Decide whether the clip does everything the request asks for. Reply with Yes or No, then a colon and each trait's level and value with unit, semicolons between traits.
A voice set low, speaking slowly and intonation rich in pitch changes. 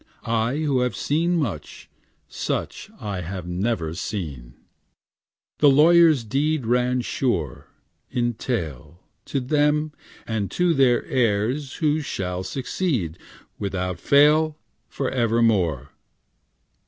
Yes: low, 120 Hz; slow, 105 wpm; wide, 7.8 semitones